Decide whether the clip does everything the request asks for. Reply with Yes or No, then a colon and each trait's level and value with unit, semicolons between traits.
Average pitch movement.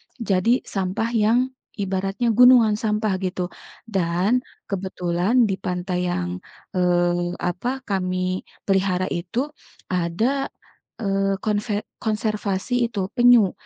Yes: average, 3.7 semitones